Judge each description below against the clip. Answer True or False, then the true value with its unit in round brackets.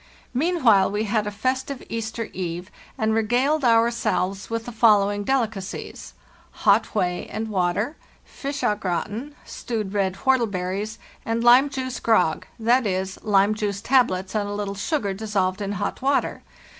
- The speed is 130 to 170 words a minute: True (145 wpm)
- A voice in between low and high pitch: False (215 Hz)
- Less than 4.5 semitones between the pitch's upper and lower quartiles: True (3.4 semitones)